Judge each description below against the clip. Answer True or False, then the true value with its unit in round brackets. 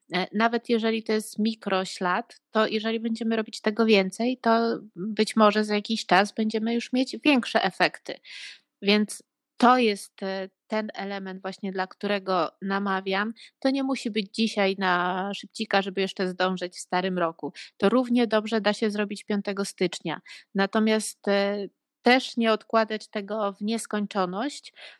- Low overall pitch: False (210 Hz)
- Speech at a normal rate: True (140 wpm)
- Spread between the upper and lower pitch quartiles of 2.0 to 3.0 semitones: True (2.7 semitones)